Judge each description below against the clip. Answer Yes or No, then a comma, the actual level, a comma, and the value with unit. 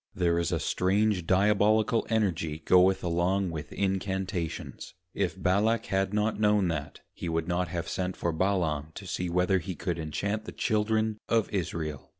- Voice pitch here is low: Yes, very low, 95 Hz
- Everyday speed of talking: Yes, average, 160 wpm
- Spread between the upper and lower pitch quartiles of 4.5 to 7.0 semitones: No, average, 3.3 semitones